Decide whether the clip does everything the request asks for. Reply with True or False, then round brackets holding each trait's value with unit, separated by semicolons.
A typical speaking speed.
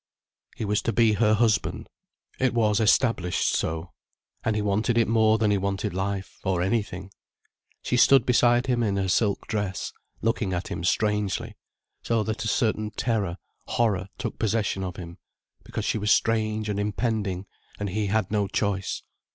True (170 wpm)